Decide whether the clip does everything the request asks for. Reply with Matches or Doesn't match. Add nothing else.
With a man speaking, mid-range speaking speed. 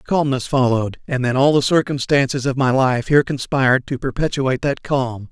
Matches